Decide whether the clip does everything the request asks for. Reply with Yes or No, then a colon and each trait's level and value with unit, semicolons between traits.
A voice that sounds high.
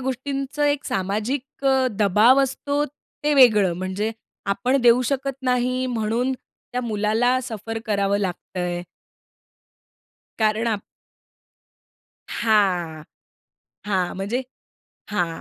Yes: high, 225 Hz